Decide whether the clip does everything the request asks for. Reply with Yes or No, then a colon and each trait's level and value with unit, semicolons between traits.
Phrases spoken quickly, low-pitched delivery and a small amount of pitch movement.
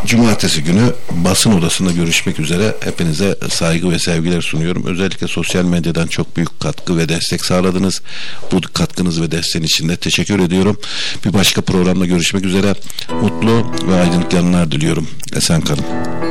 Yes: fast, 145 wpm; very low, 90 Hz; narrow, 2.0 semitones